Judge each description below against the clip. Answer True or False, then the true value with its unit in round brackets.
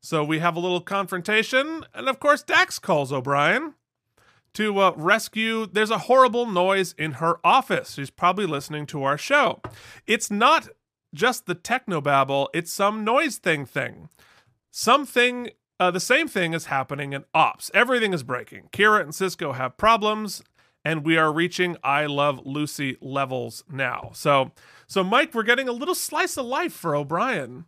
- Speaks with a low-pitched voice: False (180 Hz)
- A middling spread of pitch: False (7.8 semitones)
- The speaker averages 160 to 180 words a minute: True (165 wpm)